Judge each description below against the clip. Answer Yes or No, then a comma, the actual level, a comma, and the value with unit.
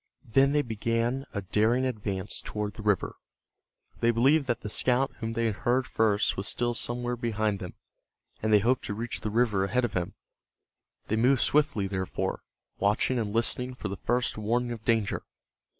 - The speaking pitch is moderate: No, low, 115 Hz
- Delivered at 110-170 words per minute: No, average, 180 wpm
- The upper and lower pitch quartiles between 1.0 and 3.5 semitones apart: Yes, average, 2.8 semitones